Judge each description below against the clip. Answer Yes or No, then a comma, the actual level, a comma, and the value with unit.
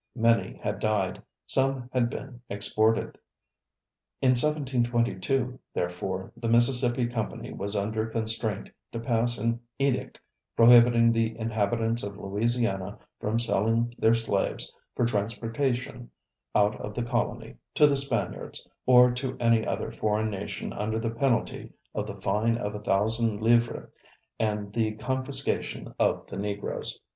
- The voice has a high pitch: No, low, 115 Hz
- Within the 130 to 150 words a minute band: Yes, slow, 135 wpm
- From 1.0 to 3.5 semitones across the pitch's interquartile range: Yes, narrow, 2.4 semitones